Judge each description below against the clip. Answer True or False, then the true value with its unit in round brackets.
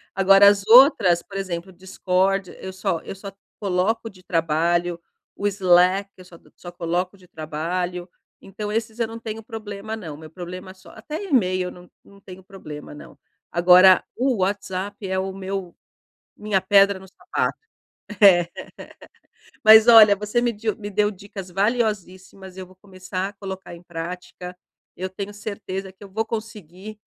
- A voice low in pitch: False (190 Hz)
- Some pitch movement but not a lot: False (2.3 semitones)